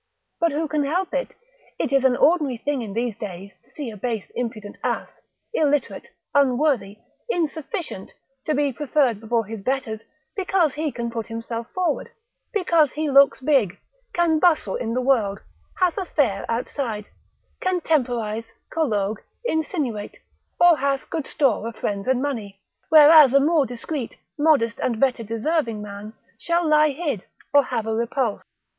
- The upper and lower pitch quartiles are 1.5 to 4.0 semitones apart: No, wide, 5.4 semitones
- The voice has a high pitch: Yes, very high, 265 Hz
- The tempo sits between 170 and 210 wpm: No, average, 155 wpm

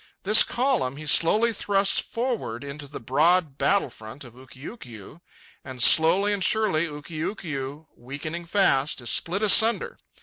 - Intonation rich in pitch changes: Yes, wide, 6.8 semitones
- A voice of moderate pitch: Yes, medium, 160 Hz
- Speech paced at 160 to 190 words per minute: No, slow, 135 wpm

